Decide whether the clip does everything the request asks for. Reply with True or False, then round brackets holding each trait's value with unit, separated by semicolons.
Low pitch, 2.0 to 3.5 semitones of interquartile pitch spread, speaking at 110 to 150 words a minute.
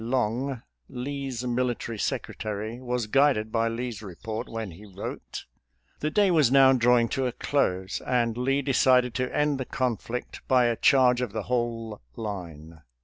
False (120 Hz; 2.9 semitones; 165 wpm)